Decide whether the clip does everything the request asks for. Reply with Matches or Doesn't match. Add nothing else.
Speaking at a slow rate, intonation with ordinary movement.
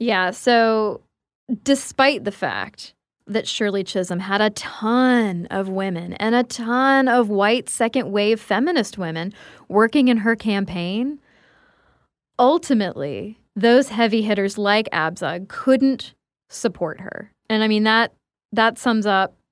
Matches